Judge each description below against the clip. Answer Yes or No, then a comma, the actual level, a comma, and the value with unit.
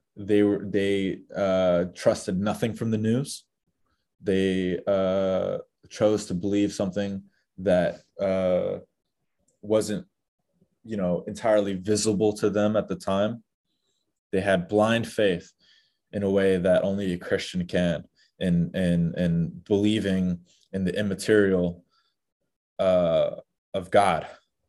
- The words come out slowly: Yes, slow, 120 wpm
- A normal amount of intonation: No, narrow, 2.3 semitones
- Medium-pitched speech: No, low, 100 Hz